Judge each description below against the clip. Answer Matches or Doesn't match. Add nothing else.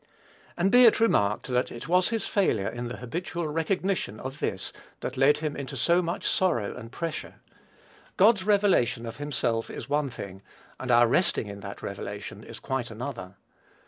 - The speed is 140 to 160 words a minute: Doesn't match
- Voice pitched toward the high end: Doesn't match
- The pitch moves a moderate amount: Doesn't match